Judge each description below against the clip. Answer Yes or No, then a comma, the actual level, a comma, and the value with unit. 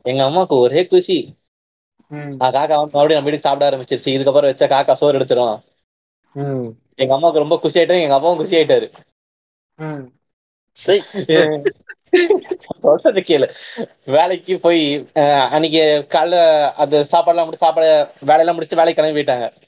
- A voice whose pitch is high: No, medium, 155 Hz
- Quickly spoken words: No, average, 120 wpm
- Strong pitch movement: No, average, 3.7 semitones